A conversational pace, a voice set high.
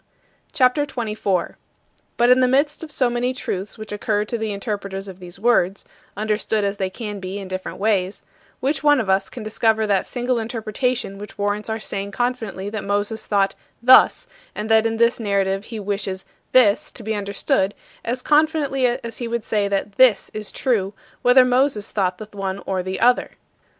Yes: average, 185 wpm; high, 215 Hz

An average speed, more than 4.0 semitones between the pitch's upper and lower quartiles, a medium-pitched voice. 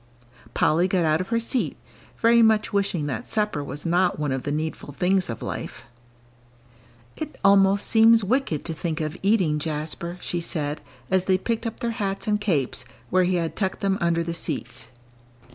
Yes: average, 180 wpm; average, 4.9 semitones; medium, 180 Hz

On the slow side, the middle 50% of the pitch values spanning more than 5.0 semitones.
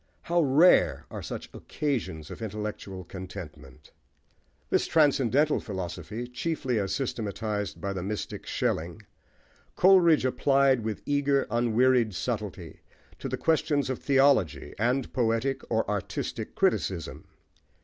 Yes: slow, 120 wpm; wide, 5.6 semitones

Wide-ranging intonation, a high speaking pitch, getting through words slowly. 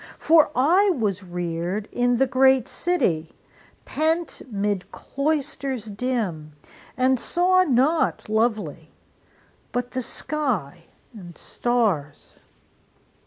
Yes: wide, 6.8 semitones; high, 245 Hz; slow, 95 wpm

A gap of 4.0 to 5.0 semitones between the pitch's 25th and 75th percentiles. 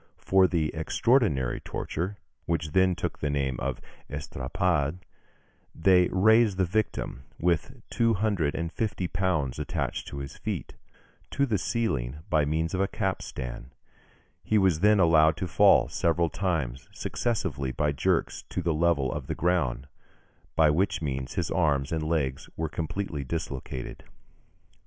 Yes: average, 4.6 semitones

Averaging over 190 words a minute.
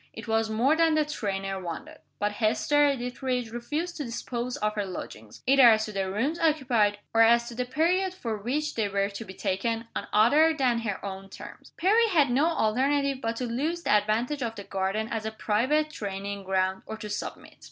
Yes: fast, 205 wpm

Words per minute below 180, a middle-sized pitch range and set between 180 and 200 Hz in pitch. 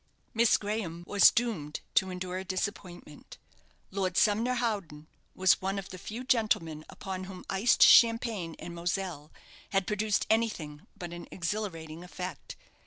Yes: average, 140 wpm; average, 3.8 semitones; high, 190 Hz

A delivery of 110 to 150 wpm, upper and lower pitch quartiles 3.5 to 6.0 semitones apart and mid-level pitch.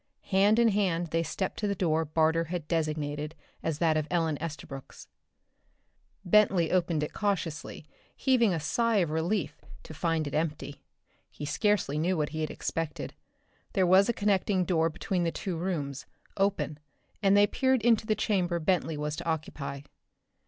No: average, 165 wpm; average, 4.1 semitones; medium, 165 Hz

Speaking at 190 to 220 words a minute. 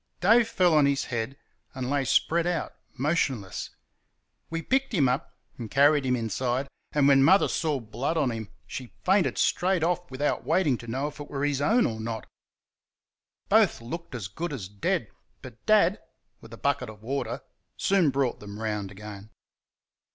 No: average, 175 wpm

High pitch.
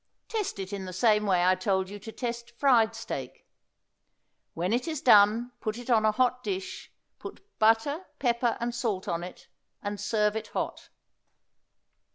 Yes: high, 220 Hz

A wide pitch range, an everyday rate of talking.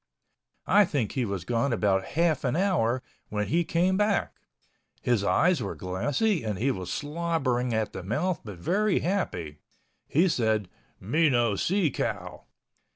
Yes: wide, 8.3 semitones; average, 155 wpm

